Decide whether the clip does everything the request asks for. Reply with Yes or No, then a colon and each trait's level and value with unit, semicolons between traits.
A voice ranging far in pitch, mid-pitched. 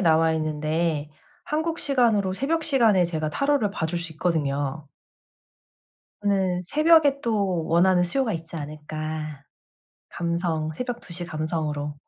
Yes: wide, 5.9 semitones; medium, 170 Hz